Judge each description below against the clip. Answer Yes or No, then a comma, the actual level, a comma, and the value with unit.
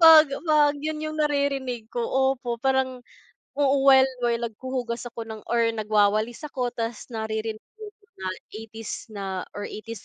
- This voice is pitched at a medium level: No, high, 240 Hz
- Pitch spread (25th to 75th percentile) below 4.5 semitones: Yes, average, 4.1 semitones